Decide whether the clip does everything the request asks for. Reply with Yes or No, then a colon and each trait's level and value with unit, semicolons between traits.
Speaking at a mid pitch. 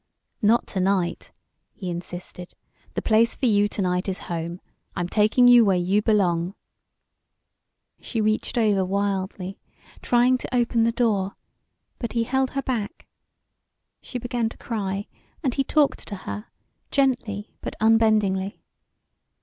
No: high, 210 Hz